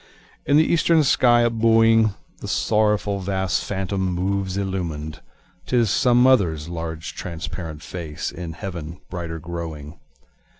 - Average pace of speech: No, slow, 125 wpm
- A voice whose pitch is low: Yes, very low, 95 Hz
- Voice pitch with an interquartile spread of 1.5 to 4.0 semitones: No, average, 5.1 semitones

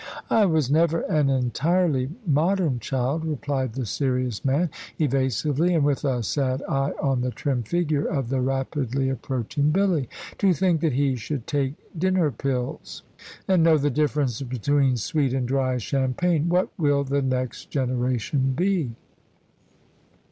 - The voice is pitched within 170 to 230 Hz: No, medium, 140 Hz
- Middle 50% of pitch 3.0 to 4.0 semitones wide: Yes, average, 3.4 semitones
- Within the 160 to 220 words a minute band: No, average, 145 wpm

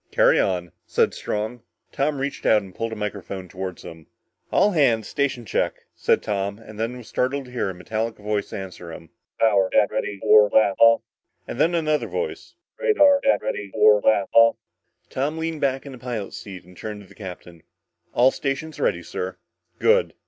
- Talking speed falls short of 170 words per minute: No, average, 185 wpm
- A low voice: Yes, low, 110 Hz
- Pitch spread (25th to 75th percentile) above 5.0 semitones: Yes, wide, 5.5 semitones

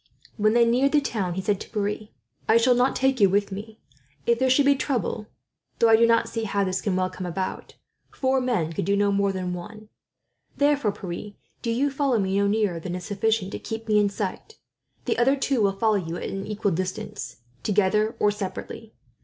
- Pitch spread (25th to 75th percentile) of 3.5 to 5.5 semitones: No, average, 3.1 semitones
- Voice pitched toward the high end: Yes, high, 210 Hz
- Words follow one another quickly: Yes, fast, 215 wpm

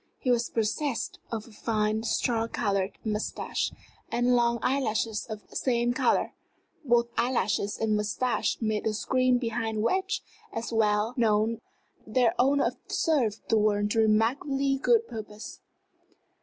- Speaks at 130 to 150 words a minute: Yes, average, 140 wpm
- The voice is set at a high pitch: Yes, high, 230 Hz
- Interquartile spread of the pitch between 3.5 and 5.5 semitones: No, narrow, 2.6 semitones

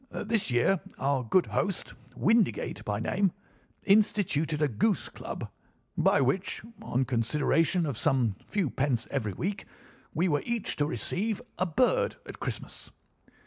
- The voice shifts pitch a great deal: Yes, wide, 7.3 semitones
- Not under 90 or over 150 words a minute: Yes, average, 140 wpm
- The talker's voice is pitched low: No, medium, 155 Hz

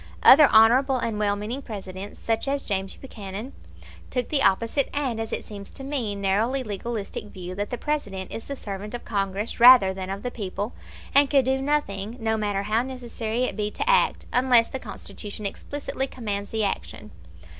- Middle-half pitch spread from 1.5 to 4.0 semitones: No, average, 4.5 semitones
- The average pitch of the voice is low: No, high, 225 Hz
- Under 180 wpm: No, average, 185 wpm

